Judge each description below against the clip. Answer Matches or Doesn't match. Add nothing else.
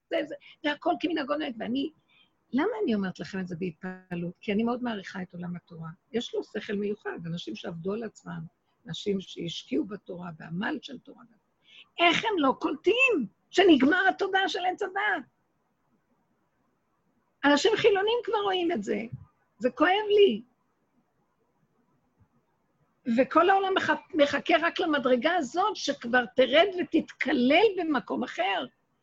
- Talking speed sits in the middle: Matches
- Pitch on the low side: Doesn't match